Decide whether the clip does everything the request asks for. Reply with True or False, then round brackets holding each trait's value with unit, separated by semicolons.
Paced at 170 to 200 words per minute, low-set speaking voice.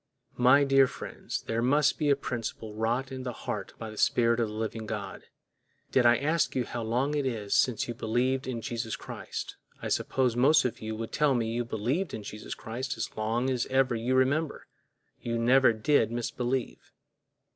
True (190 wpm; 120 Hz)